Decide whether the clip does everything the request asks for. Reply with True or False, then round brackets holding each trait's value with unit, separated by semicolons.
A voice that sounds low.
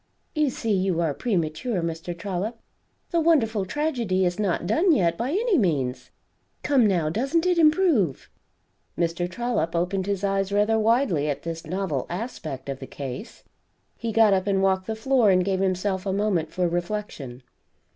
False (195 Hz)